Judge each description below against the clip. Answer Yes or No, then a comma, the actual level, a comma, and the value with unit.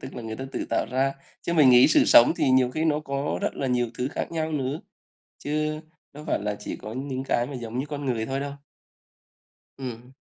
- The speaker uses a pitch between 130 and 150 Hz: Yes, low, 135 Hz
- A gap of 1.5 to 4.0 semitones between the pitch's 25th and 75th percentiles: Yes, average, 2.9 semitones